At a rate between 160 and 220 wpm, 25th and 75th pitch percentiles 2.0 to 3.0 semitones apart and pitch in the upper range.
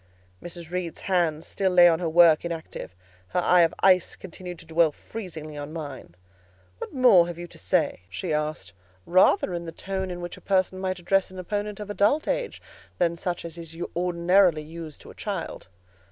No: average, 190 wpm; narrow, 2.4 semitones; medium, 175 Hz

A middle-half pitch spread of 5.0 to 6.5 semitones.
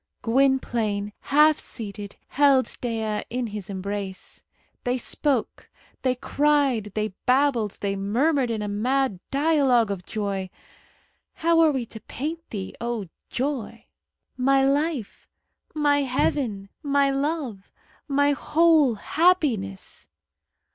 Yes: average, 5.3 semitones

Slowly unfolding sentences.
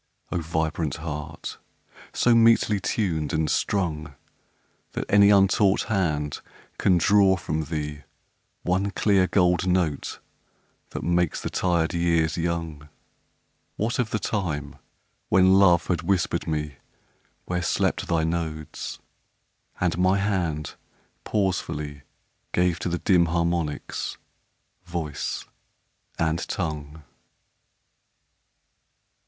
Yes: slow, 105 wpm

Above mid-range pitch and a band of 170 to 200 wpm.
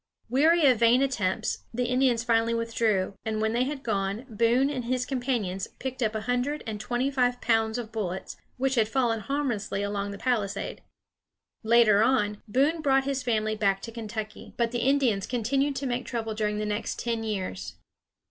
Yes: high, 230 Hz; average, 180 wpm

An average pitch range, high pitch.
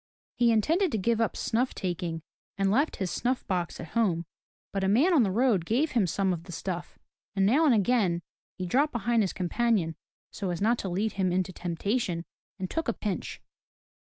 Yes: average, 4.8 semitones; high, 200 Hz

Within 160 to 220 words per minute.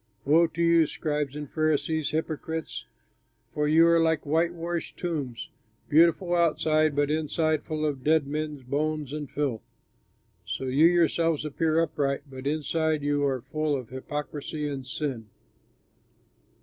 No: slow, 135 wpm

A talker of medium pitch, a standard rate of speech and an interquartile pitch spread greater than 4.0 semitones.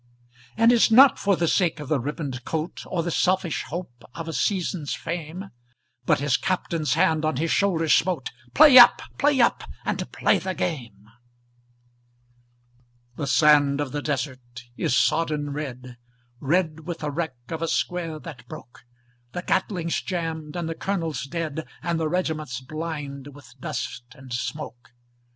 No: medium, 160 Hz; average, 155 wpm; average, 3.6 semitones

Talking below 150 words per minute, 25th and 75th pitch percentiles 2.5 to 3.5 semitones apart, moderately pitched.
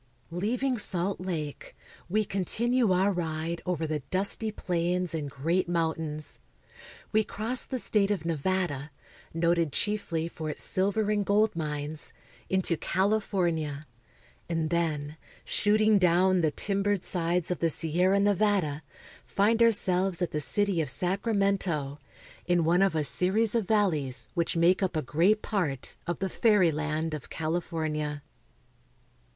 No: slow, 135 wpm; average, 4.1 semitones; medium, 175 Hz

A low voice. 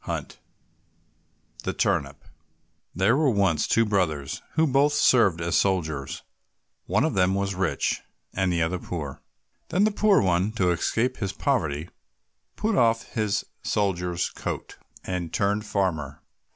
Yes: very low, 95 Hz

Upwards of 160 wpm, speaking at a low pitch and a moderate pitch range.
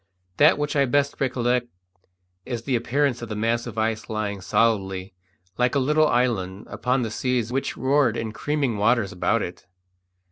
Yes: average, 170 wpm; low, 120 Hz; average, 3.6 semitones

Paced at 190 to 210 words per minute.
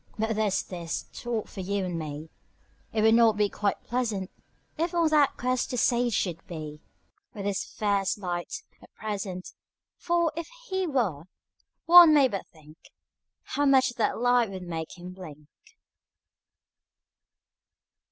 No: average, 145 wpm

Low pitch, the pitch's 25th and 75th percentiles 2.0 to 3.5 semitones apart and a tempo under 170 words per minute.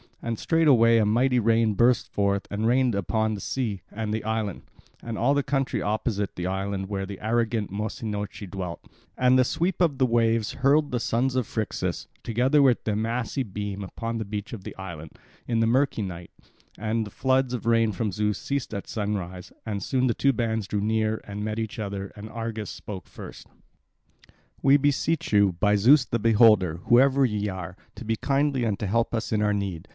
No: low, 110 Hz; average, 3.2 semitones; average, 195 wpm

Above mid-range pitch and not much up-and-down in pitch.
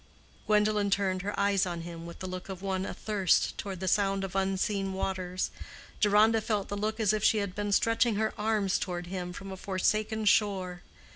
Yes: high, 195 Hz; narrow, 2.1 semitones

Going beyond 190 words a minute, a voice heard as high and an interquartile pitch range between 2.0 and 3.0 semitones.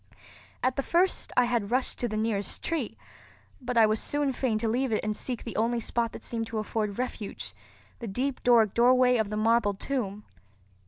Yes: average, 200 wpm; high, 230 Hz; average, 2.7 semitones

